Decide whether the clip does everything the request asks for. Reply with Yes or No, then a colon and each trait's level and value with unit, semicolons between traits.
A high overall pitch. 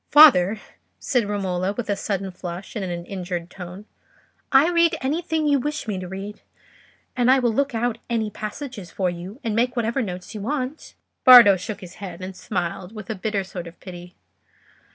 Yes: high, 210 Hz